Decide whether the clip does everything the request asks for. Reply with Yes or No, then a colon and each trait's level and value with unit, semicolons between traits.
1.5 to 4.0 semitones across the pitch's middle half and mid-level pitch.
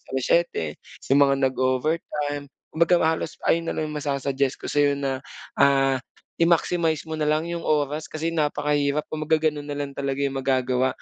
Yes: narrow, 2.4 semitones; medium, 145 Hz